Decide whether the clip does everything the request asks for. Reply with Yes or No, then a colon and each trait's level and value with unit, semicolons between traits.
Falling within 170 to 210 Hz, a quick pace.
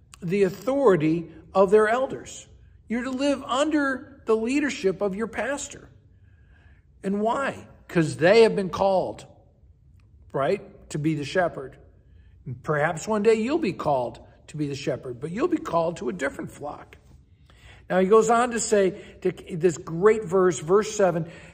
No: high, 190 Hz; average, 160 wpm